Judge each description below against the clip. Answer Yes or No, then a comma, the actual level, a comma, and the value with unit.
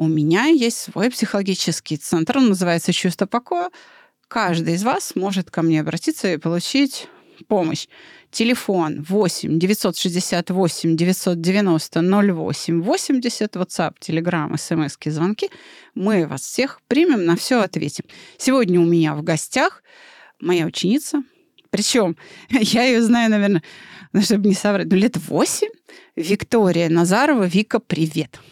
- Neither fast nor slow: Yes, average, 125 wpm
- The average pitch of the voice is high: Yes, high, 195 Hz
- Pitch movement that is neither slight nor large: No, wide, 6.1 semitones